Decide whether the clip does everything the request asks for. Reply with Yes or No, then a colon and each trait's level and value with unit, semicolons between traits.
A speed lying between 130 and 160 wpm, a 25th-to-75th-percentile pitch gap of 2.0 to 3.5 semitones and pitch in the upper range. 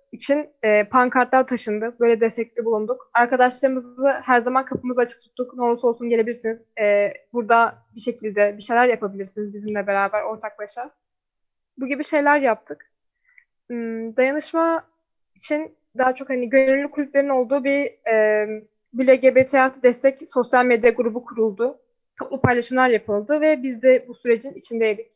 Yes: average, 135 wpm; average, 2.9 semitones; high, 245 Hz